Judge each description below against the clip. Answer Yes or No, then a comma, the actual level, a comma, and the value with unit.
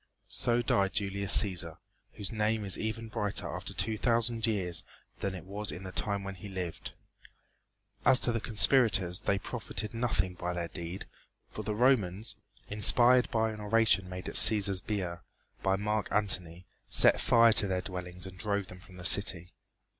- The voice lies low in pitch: Yes, low, 100 Hz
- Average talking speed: Yes, average, 170 wpm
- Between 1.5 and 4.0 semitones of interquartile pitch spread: Yes, average, 3.2 semitones